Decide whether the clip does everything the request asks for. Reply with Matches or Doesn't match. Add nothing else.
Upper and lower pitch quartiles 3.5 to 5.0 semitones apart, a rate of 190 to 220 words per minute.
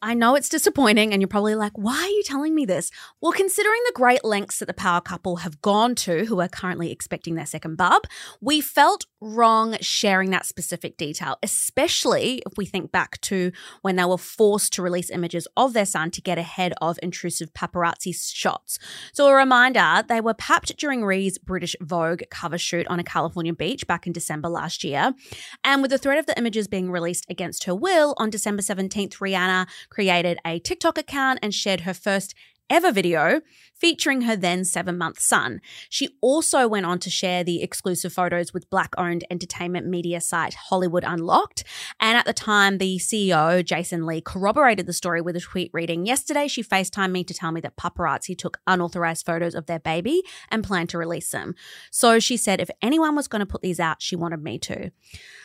Matches